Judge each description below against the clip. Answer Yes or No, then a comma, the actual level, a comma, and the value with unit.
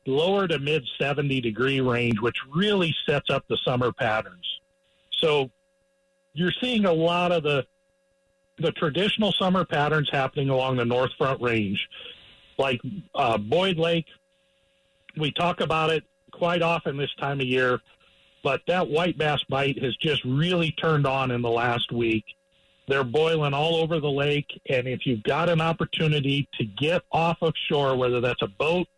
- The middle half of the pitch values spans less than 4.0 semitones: No, average, 5.0 semitones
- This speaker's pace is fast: No, average, 165 wpm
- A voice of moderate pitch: Yes, medium, 145 Hz